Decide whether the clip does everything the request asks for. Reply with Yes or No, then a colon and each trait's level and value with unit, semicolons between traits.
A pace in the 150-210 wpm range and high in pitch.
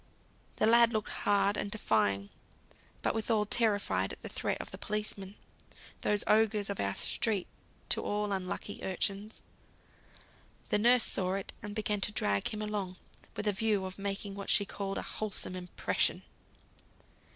Yes: average, 155 wpm; high, 205 Hz